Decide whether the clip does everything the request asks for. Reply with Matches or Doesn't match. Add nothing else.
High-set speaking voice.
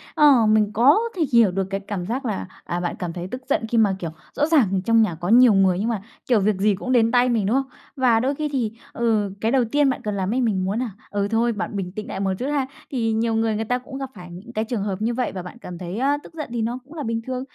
Matches